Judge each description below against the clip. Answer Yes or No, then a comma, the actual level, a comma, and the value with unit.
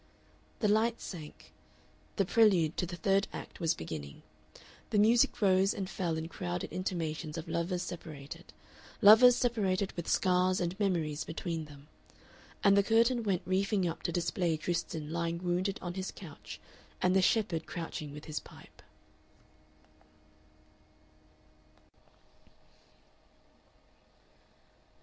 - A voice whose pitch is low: No, medium, 180 Hz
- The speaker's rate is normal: No, slow, 120 wpm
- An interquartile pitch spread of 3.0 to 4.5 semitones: Yes, average, 3.4 semitones